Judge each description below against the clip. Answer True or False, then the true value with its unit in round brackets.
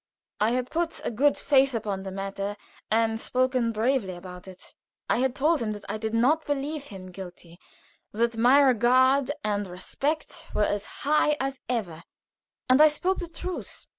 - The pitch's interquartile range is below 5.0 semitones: False (5.4 semitones)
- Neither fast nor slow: True (170 wpm)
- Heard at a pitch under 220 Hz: False (240 Hz)